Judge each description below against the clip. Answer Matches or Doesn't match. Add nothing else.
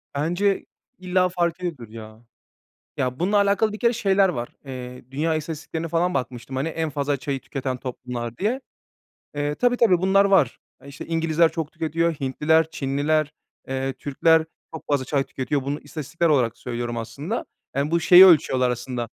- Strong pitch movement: Doesn't match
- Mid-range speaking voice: Matches